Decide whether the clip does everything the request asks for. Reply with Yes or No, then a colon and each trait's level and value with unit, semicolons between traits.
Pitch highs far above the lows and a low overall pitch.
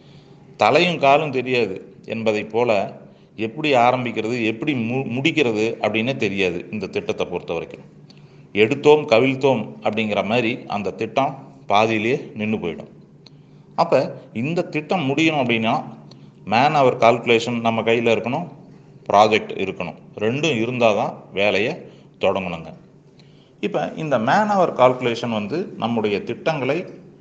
No: average, 3.7 semitones; low, 115 Hz